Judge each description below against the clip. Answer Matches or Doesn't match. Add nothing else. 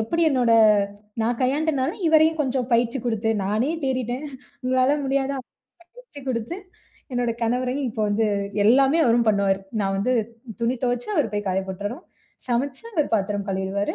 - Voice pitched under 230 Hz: Doesn't match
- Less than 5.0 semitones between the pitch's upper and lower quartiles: Matches